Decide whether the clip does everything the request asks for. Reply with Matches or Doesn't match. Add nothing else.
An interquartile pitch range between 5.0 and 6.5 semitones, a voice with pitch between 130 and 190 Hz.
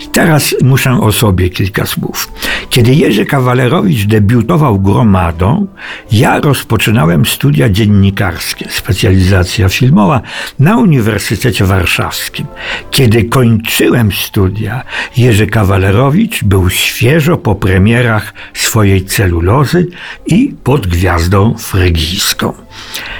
Doesn't match